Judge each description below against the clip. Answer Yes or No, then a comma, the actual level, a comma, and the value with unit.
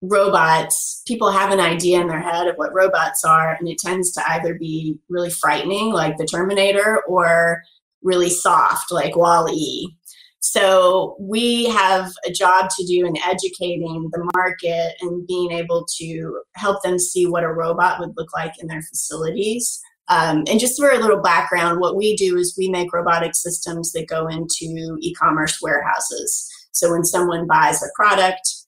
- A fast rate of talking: No, average, 170 wpm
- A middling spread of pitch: No, narrow, 2.3 semitones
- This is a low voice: No, medium, 175 Hz